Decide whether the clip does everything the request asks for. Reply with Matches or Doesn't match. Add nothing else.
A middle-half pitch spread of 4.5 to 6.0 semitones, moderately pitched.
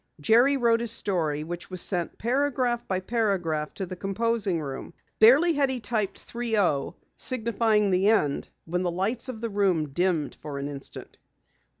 Doesn't match